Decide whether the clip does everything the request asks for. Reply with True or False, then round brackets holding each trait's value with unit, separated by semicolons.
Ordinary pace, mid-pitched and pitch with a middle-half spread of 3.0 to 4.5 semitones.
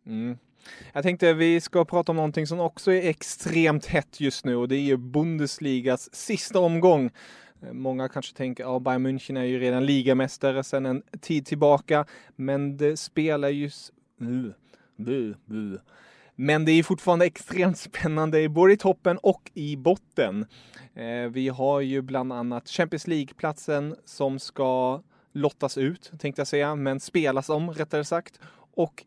True (150 wpm; 145 Hz; 4.0 semitones)